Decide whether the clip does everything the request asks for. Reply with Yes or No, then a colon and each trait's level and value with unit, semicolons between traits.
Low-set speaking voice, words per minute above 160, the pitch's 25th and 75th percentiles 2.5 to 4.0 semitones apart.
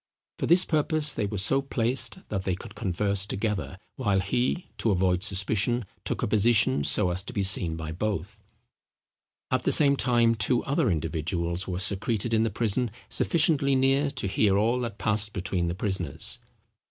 No: low, 105 Hz; average, 175 wpm; average, 4.7 semitones